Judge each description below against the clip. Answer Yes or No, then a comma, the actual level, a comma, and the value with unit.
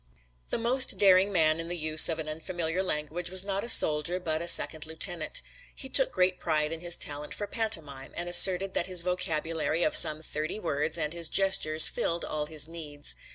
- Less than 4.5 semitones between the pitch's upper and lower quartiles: Yes, average, 3.0 semitones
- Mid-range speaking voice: Yes, medium, 165 Hz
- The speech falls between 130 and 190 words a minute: No, average, 200 wpm